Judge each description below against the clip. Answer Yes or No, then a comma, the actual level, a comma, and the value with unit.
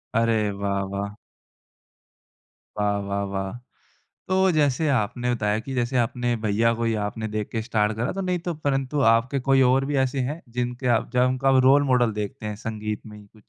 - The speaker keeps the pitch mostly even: No, average, 3.6 semitones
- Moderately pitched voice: No, low, 115 Hz